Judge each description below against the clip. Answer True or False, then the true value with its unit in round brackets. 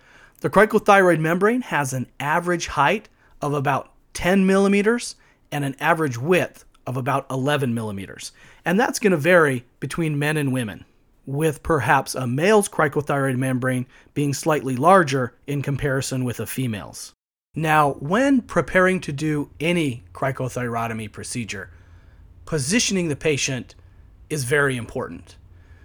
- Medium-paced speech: False (130 wpm)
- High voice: False (140 Hz)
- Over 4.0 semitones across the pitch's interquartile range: True (5.3 semitones)